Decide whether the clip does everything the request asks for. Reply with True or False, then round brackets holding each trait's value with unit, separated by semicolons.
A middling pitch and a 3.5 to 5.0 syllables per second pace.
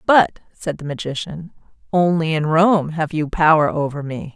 True (160 Hz; 4.7 syllables/s)